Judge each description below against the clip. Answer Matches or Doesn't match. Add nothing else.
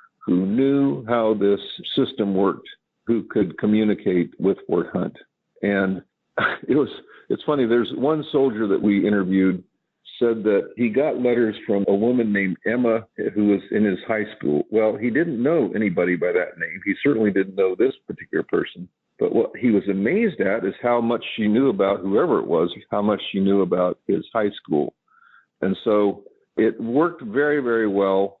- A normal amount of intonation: Matches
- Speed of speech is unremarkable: Matches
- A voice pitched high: Doesn't match